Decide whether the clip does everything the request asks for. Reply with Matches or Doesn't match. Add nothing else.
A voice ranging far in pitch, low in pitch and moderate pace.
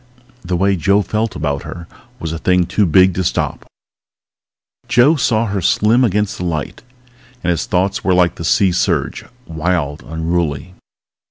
Doesn't match